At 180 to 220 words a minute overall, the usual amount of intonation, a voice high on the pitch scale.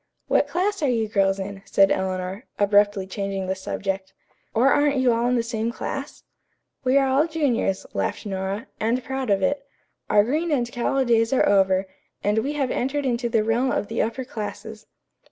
Yes: average, 190 wpm; average, 5.0 semitones; high, 230 Hz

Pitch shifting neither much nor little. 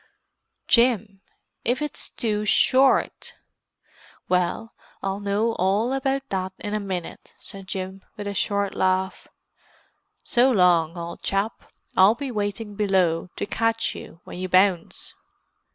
Yes: average, 3.3 semitones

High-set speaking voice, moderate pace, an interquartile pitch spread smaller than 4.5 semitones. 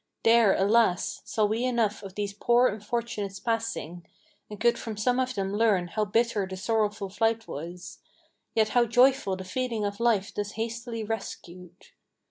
Yes: high, 215 Hz; average, 160 wpm; average, 2.9 semitones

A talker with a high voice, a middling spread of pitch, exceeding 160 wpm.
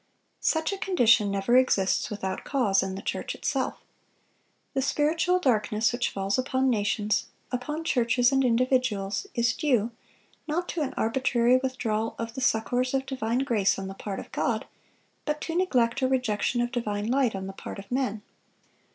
Yes: high, 240 Hz; average, 4.0 semitones; average, 170 wpm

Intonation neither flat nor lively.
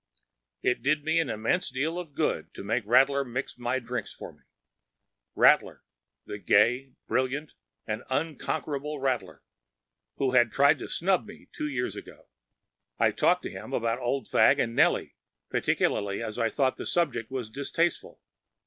Yes: average, 3.8 semitones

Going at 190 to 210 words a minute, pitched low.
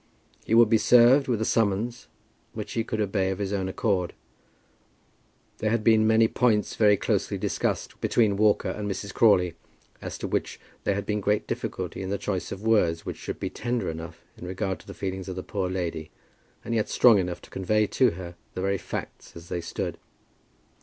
Yes: average, 200 wpm; low, 100 Hz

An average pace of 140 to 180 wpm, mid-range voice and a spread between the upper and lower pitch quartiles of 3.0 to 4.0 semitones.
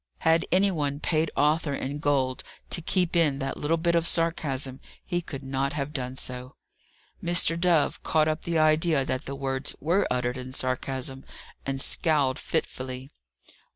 Yes: average, 160 wpm; medium, 145 Hz; average, 3.7 semitones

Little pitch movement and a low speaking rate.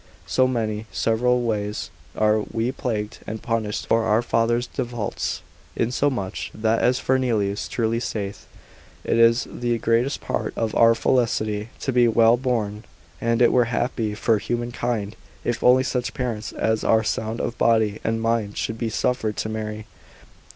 No: narrow, 1.9 semitones; average, 160 wpm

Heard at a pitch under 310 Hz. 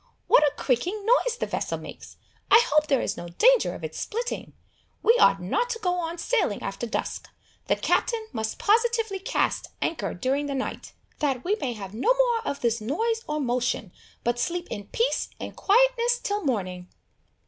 No: very high, 325 Hz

